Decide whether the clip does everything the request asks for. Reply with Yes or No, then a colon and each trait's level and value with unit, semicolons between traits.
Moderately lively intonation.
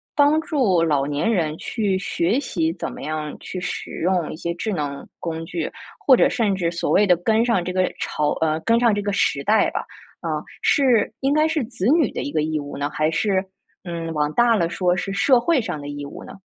No: wide, 6.5 semitones